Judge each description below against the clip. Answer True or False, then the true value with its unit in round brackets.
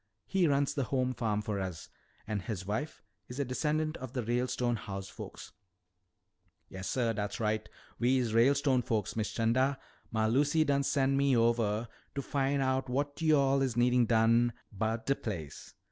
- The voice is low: True (125 Hz)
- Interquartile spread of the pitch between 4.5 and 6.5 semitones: False (3.9 semitones)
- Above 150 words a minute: True (165 wpm)